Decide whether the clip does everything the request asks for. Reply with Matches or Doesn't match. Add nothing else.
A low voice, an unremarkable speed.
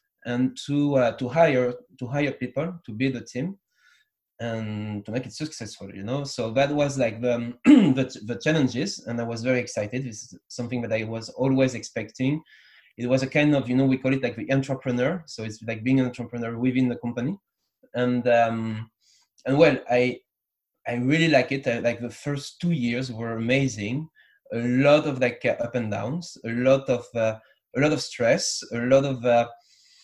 Matches